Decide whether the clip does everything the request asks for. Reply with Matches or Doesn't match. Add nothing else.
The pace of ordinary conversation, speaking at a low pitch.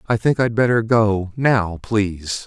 Matches